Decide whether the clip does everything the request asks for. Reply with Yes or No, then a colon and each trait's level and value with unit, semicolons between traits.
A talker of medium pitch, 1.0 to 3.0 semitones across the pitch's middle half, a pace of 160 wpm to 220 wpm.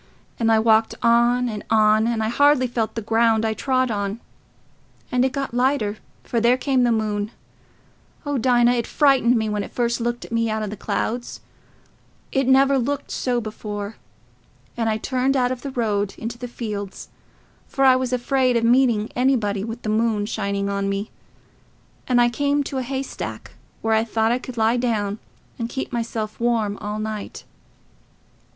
No: high, 235 Hz; narrow, 2.6 semitones; average, 175 wpm